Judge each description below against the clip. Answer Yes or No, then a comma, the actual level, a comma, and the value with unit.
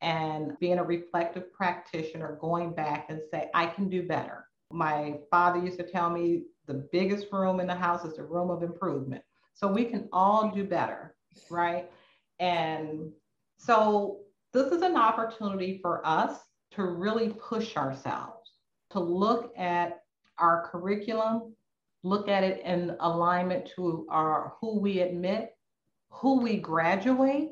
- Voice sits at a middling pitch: Yes, medium, 180 Hz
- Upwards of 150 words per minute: No, average, 145 wpm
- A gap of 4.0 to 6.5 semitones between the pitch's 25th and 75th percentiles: No, average, 3.2 semitones